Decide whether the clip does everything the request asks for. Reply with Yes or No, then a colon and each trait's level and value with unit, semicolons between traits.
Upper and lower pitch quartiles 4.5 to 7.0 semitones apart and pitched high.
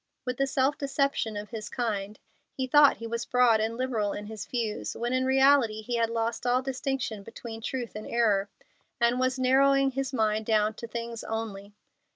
No: average, 3.1 semitones; high, 235 Hz